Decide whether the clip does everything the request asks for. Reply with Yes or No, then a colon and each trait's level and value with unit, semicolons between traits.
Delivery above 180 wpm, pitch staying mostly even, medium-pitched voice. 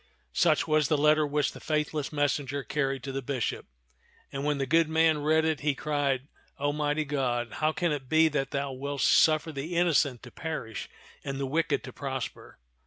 Yes: average, 190 wpm; narrow, 2.1 semitones; medium, 145 Hz